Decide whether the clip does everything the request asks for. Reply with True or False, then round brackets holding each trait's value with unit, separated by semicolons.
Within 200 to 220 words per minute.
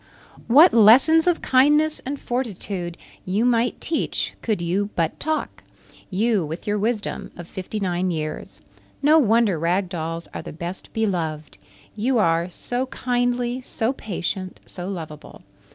False (140 wpm)